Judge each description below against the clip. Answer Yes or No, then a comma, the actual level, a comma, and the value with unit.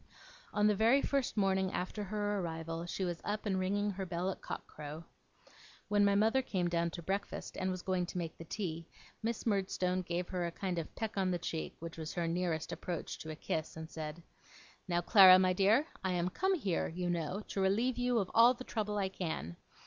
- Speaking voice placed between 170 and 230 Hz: Yes, medium, 185 Hz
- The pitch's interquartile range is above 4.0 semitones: No, average, 3.3 semitones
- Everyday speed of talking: No, fast, 215 wpm